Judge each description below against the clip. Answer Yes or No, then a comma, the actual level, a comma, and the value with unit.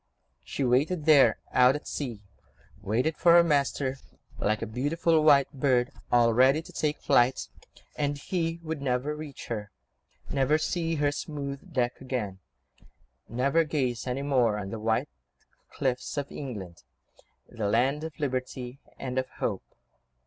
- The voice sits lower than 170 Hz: Yes, low, 135 Hz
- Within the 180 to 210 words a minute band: No, average, 145 wpm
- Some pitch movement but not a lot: Yes, average, 3.5 semitones